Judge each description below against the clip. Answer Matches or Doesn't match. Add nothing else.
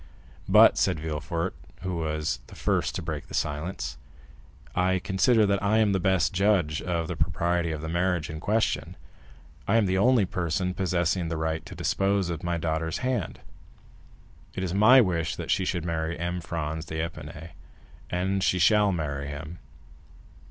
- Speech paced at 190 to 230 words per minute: Doesn't match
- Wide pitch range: Doesn't match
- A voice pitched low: Matches